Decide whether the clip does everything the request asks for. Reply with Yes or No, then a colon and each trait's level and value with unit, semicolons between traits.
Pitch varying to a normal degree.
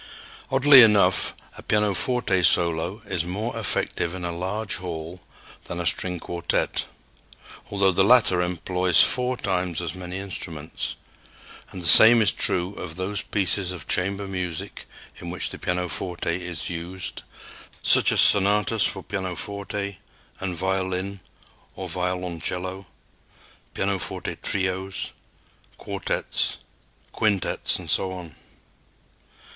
No: narrow, 2.1 semitones